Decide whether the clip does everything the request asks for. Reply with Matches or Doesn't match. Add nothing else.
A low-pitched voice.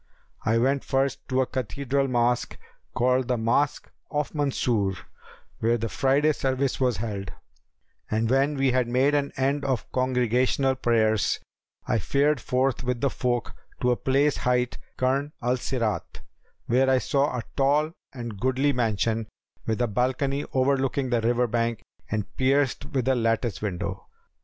Matches